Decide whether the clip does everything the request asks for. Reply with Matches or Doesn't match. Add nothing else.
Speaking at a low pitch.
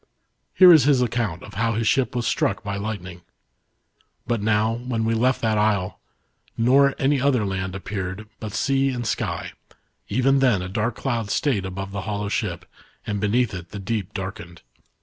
Matches